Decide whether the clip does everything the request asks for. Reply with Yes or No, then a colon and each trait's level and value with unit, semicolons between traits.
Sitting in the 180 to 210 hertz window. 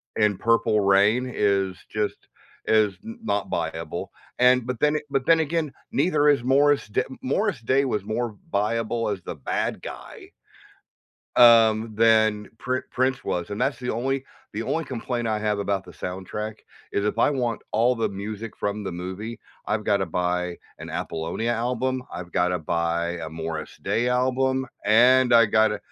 No: low, 110 Hz